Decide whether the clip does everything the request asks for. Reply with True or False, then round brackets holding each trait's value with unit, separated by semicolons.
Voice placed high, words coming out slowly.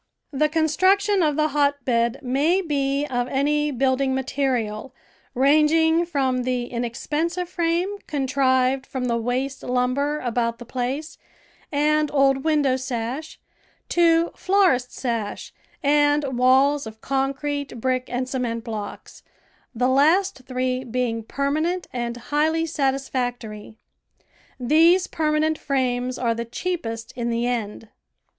True (270 Hz; 120 wpm)